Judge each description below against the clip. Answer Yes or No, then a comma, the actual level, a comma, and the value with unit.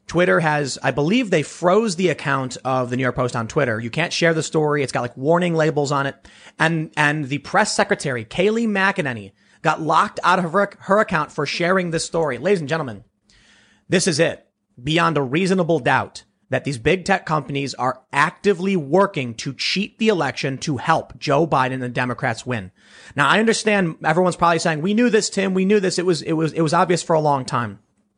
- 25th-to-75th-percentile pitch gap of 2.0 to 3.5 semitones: No, average, 5.2 semitones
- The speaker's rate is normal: No, fast, 210 wpm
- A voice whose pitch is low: No, medium, 160 Hz